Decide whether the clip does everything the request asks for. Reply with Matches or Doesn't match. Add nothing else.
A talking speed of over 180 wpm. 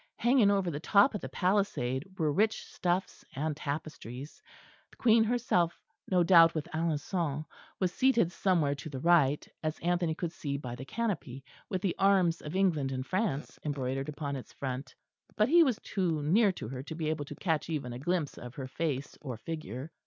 Matches